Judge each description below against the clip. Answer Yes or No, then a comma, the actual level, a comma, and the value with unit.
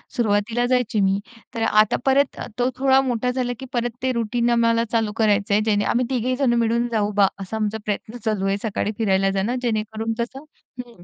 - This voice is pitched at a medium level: No, high, 230 Hz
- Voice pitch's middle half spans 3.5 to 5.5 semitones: No, average, 2.7 semitones